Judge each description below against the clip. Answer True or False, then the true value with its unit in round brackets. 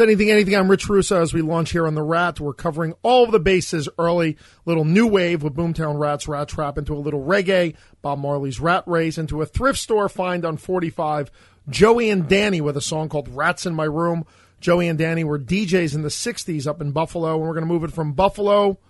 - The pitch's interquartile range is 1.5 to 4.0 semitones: True (3.7 semitones)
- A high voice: False (165 Hz)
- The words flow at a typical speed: False (225 wpm)